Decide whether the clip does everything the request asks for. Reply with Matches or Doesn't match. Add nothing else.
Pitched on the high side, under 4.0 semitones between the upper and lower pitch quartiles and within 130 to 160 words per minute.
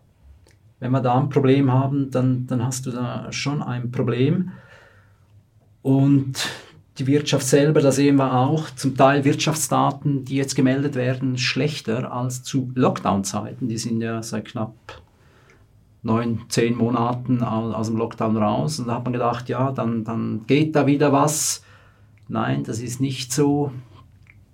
Doesn't match